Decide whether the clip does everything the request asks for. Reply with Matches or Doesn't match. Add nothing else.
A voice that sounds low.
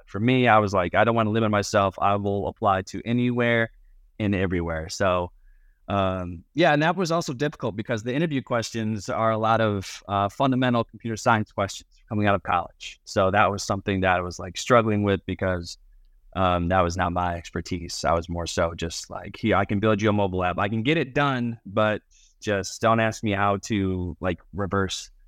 Matches